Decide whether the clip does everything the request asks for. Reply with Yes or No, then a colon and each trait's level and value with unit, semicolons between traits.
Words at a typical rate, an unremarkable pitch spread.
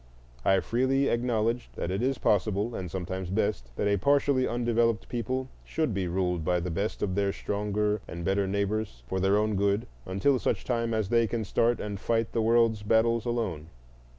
Yes: average, 185 wpm; average, 3.4 semitones